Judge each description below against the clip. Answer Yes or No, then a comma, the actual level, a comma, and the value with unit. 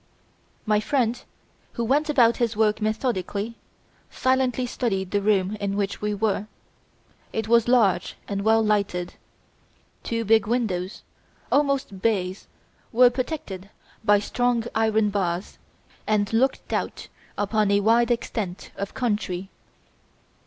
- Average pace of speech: No, slow, 125 wpm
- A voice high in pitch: Yes, high, 215 Hz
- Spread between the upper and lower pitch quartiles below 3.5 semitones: Yes, average, 3.0 semitones